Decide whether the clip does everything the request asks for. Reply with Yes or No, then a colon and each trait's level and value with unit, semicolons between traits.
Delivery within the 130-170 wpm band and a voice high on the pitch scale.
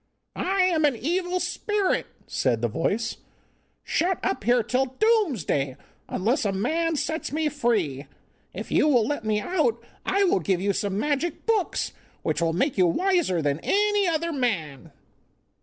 Yes: average, 155 wpm; very high, 265 Hz